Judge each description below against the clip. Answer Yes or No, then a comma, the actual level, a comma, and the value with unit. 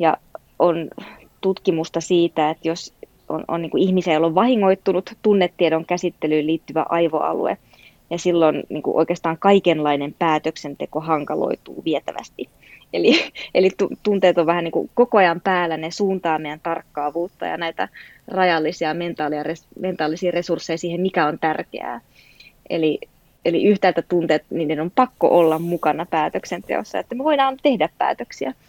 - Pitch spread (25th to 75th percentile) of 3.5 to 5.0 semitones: No, average, 2.8 semitones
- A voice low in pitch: No, medium, 170 Hz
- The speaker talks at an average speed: Yes, average, 130 wpm